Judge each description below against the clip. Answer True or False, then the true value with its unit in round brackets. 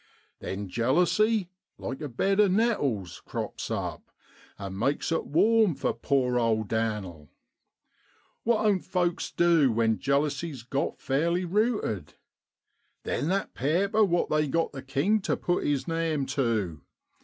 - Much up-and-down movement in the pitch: True (7.7 semitones)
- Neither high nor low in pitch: True (145 Hz)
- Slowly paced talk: True (130 wpm)